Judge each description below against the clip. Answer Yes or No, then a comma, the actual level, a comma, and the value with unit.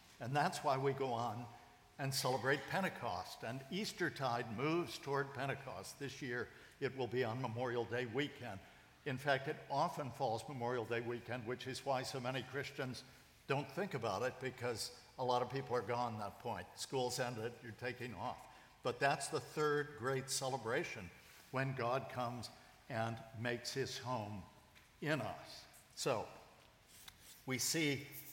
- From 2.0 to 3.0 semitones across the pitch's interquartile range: Yes, narrow, 2.5 semitones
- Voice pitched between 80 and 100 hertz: No, low, 130 Hz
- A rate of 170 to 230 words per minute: No, average, 160 wpm